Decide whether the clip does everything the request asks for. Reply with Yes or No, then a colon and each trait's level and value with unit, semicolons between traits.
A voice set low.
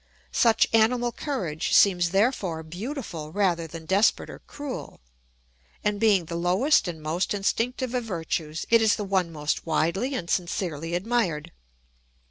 No: high, 190 Hz